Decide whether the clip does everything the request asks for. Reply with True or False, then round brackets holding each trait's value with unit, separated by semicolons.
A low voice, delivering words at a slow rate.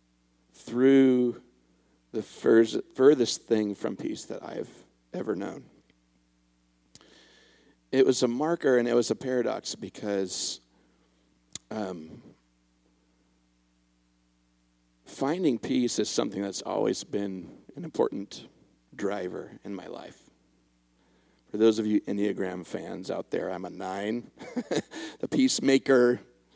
True (90 Hz; 110 wpm)